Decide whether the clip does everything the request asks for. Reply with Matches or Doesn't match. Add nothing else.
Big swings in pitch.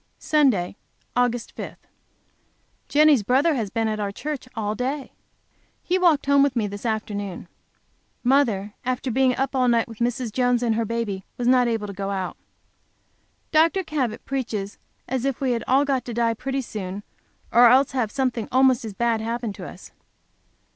Doesn't match